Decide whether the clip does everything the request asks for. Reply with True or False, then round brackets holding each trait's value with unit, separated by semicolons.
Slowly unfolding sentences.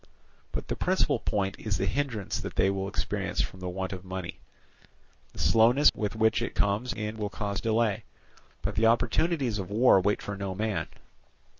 False (175 wpm)